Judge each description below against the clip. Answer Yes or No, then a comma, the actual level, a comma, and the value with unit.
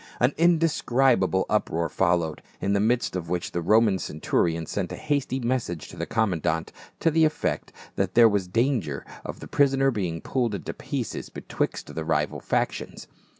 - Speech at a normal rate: Yes, average, 165 wpm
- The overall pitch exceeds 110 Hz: No, low, 105 Hz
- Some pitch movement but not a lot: No, wide, 7.0 semitones